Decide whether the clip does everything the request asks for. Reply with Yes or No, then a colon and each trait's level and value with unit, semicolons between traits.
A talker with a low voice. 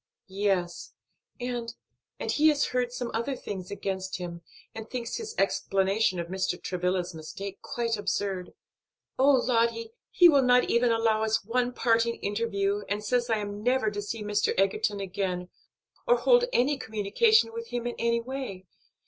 No: high, 225 Hz